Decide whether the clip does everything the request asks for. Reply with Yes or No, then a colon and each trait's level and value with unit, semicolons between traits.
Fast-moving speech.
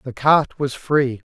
No: average, 175 wpm